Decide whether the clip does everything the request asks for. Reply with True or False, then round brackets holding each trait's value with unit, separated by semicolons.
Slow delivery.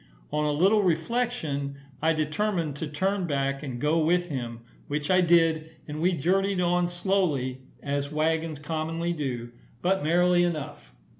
False (150 wpm)